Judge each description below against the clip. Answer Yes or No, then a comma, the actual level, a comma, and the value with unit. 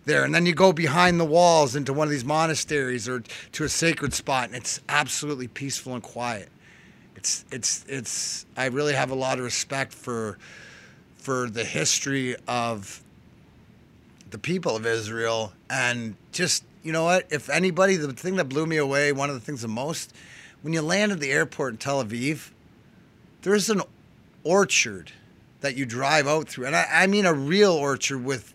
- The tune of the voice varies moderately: Yes, average, 4.4 semitones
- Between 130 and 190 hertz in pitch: Yes, medium, 140 Hz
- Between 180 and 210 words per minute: Yes, average, 185 wpm